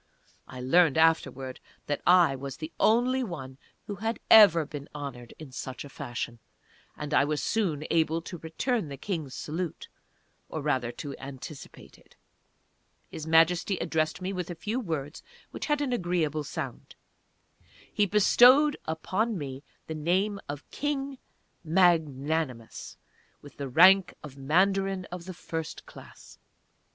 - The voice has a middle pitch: Yes, medium, 160 Hz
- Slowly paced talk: No, average, 145 wpm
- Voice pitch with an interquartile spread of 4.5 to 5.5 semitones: Yes, average, 5.0 semitones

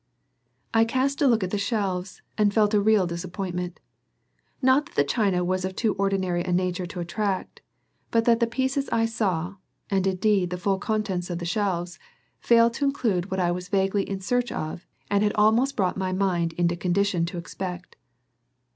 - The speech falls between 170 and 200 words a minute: Yes, average, 185 wpm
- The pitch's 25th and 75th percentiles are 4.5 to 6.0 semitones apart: No, average, 3.5 semitones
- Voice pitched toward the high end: Yes, high, 195 Hz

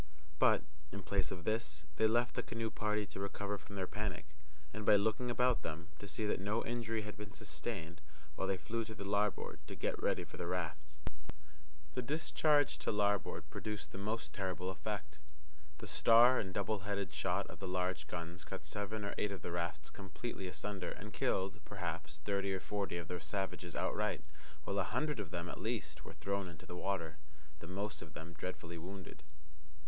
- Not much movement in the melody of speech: No, average, 3.3 semitones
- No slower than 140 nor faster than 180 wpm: No, average, 195 wpm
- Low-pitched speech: Yes, low, 100 Hz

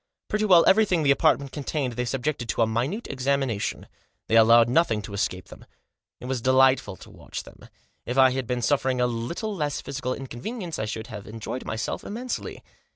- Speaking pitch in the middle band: No, low, 130 Hz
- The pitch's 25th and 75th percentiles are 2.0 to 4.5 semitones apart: Yes, average, 4.2 semitones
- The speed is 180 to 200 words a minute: Yes, average, 185 wpm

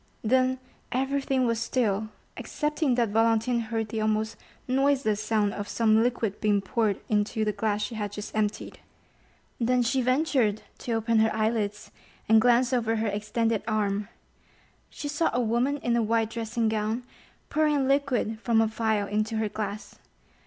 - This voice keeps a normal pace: Yes, average, 160 wpm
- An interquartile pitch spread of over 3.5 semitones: No, narrow, 2.5 semitones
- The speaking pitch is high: Yes, high, 225 Hz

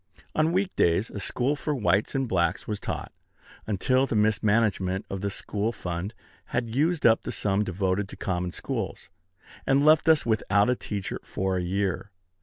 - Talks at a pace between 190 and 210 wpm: No, average, 175 wpm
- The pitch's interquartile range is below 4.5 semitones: No, average, 4.8 semitones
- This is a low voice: Yes, low, 105 Hz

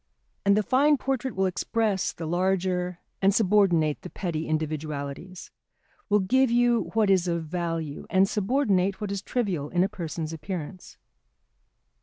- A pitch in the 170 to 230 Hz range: Yes, medium, 185 Hz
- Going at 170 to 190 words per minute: No, average, 145 wpm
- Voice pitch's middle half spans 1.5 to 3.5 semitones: No, average, 3.9 semitones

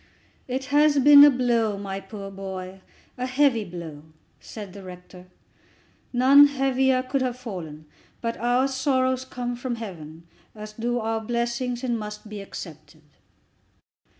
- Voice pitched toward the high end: Yes, high, 235 Hz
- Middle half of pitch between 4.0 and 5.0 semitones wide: Yes, average, 4.7 semitones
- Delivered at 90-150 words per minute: Yes, average, 140 wpm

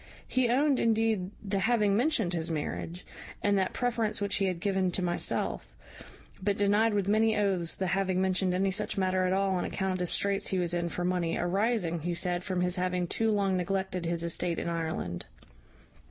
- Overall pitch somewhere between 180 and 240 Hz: Yes, high, 190 Hz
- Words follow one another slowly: No, average, 195 wpm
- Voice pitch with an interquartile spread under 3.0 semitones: Yes, narrow, 2.6 semitones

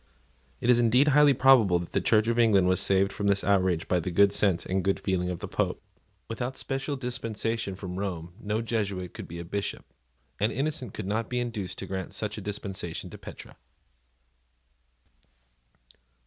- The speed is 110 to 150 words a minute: No, average, 185 wpm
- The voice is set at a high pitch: No, low, 100 Hz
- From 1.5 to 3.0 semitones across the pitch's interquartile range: No, average, 3.9 semitones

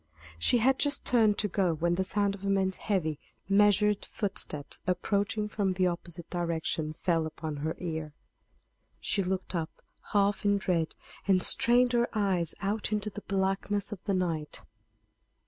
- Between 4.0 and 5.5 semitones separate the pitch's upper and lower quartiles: No, average, 3.3 semitones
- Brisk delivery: No, average, 160 wpm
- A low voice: No, high, 190 Hz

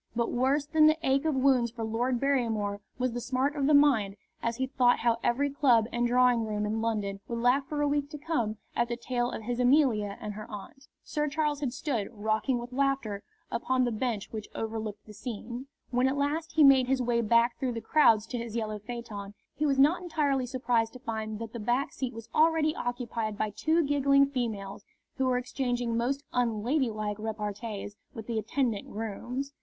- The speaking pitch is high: Yes, high, 245 Hz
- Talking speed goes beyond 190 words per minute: Yes, fast, 205 wpm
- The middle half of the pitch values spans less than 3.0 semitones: No, average, 3.7 semitones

